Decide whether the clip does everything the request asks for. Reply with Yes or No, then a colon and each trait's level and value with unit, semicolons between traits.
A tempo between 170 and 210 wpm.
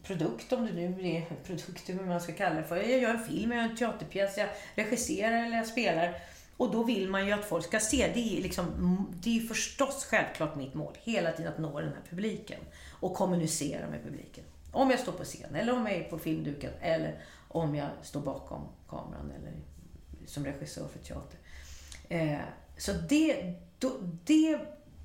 Yes: average, 190 wpm